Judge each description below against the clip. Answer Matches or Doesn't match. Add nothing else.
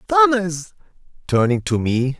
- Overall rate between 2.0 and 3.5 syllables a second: Matches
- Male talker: Matches